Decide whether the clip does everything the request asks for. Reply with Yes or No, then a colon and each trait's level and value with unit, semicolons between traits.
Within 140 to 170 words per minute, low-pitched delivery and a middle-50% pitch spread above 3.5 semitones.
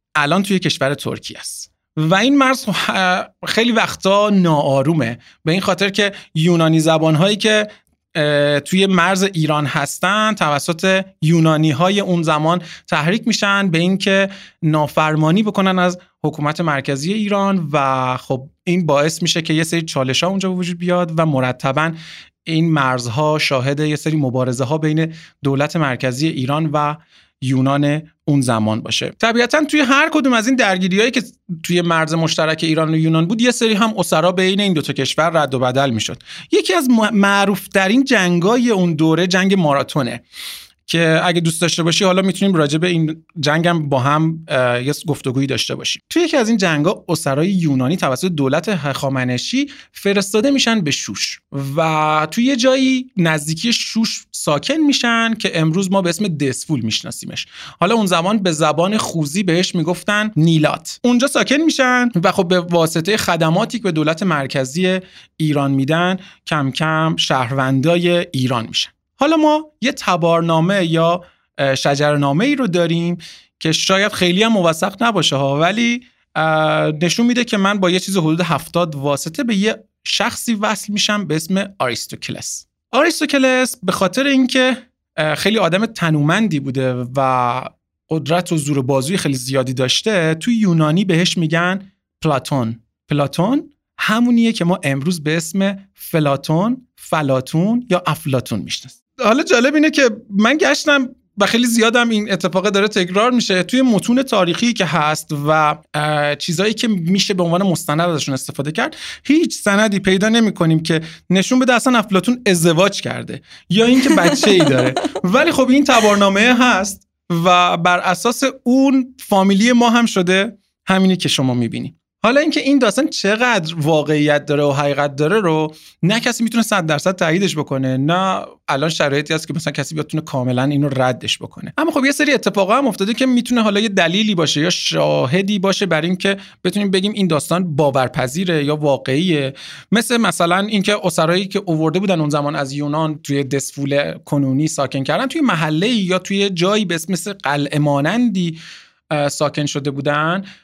No: fast, 155 wpm; medium, 175 Hz; wide, 5.5 semitones